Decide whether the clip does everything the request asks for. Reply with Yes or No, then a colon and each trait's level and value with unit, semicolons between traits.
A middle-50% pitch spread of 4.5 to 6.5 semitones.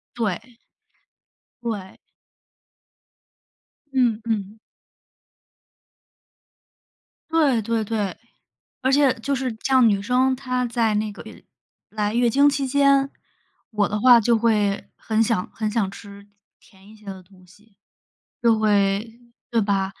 No: average, 3.5 semitones